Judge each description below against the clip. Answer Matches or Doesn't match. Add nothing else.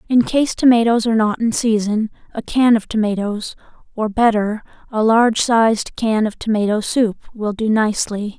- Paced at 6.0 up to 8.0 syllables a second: Doesn't match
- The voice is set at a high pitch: Matches